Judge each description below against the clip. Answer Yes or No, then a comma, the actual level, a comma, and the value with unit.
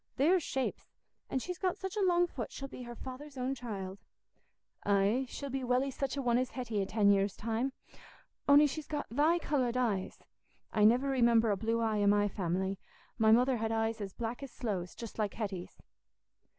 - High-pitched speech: Yes, high, 240 Hz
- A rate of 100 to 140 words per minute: No, average, 195 wpm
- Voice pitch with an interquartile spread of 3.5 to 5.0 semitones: Yes, average, 4.5 semitones